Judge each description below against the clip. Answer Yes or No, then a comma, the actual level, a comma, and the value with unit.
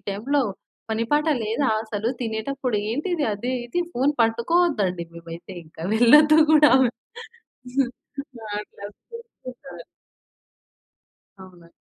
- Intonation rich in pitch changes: Yes, wide, 6.2 semitones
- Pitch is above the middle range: Yes, high, 235 Hz